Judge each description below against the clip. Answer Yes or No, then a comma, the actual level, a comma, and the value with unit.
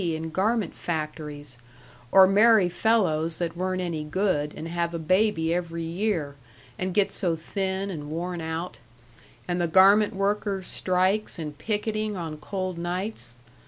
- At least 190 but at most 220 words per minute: No, average, 145 wpm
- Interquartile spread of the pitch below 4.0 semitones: Yes, average, 3.4 semitones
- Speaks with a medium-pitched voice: Yes, medium, 180 Hz